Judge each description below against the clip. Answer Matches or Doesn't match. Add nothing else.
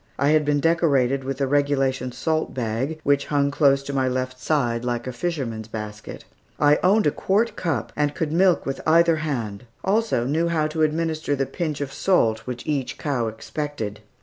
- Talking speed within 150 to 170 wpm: Doesn't match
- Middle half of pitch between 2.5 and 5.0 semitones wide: Matches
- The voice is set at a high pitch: Doesn't match